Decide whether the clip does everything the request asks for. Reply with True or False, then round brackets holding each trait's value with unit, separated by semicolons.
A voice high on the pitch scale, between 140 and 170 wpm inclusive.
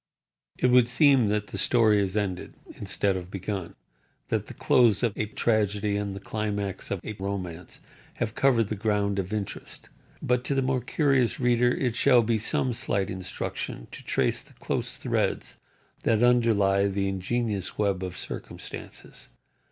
False (105 Hz; 160 wpm)